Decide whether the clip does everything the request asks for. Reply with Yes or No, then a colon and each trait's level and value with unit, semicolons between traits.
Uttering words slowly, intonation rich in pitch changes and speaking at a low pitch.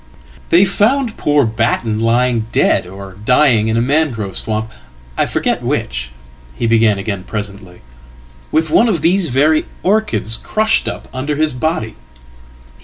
Yes: slow, 130 wpm; wide, 6.6 semitones; low, 120 Hz